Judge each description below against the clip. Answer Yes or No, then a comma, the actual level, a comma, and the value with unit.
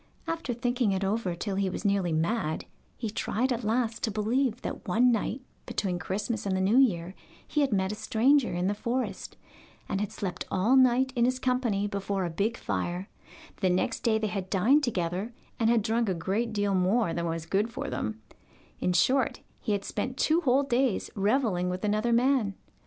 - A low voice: No, high, 215 Hz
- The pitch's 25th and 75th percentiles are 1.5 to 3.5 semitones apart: No, average, 4.4 semitones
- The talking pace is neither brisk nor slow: Yes, average, 195 wpm